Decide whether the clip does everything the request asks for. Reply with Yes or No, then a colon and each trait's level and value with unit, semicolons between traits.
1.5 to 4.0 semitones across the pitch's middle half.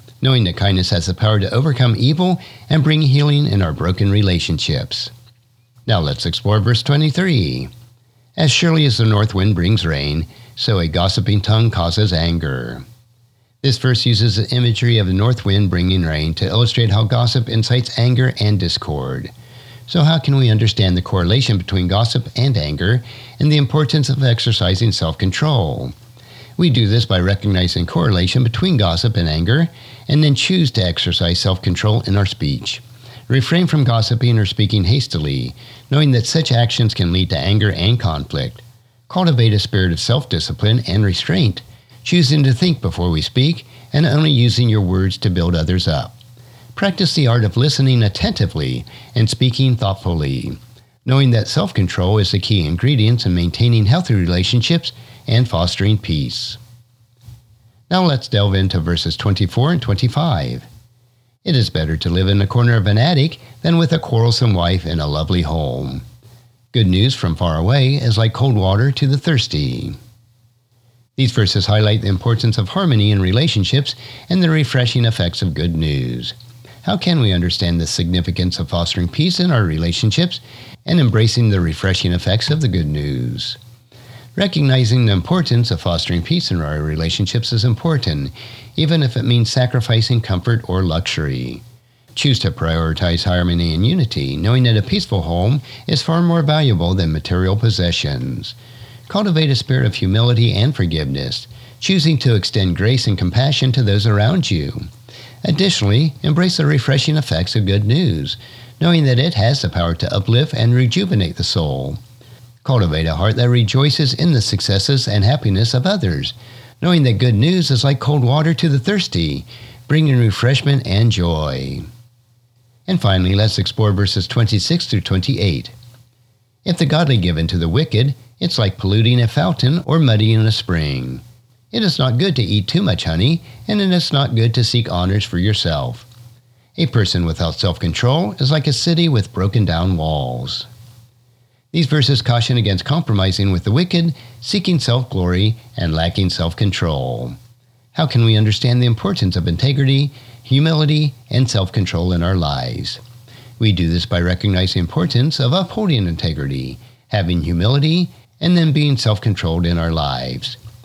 No: average, 5.3 semitones